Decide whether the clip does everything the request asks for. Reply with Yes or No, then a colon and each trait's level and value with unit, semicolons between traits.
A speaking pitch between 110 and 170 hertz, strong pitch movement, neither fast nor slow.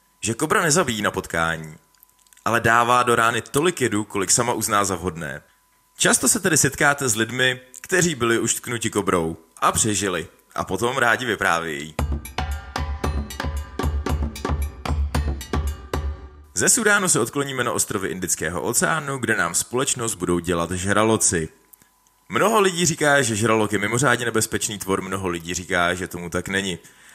No: low, 100 Hz; wide, 7.3 semitones; average, 140 wpm